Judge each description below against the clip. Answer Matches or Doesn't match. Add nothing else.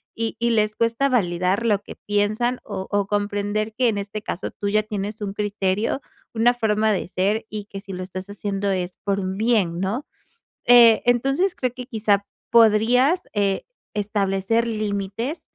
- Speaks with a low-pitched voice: Doesn't match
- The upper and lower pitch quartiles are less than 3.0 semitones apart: Matches